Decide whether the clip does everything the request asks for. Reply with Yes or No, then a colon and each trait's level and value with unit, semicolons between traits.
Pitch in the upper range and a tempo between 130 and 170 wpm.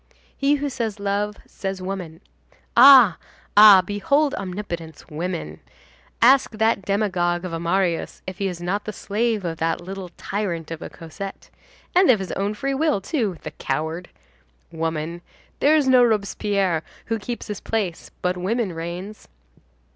Yes: high, 195 Hz; average, 150 wpm